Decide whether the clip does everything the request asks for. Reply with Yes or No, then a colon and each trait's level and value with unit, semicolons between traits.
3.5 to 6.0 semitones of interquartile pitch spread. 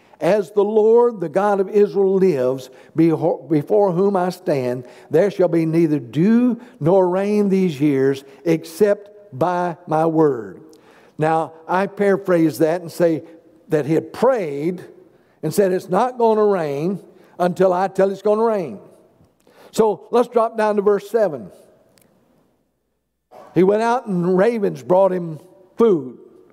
Yes: average, 4.0 semitones